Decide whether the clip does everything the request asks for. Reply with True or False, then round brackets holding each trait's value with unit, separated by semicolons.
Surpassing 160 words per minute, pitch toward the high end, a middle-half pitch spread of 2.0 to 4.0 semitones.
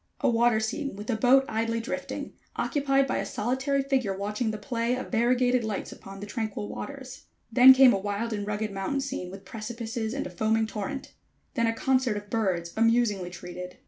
True (190 wpm; 225 Hz; 3.6 semitones)